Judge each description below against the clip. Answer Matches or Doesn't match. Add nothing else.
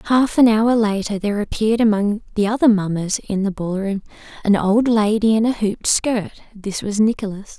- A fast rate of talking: Doesn't match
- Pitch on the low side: Doesn't match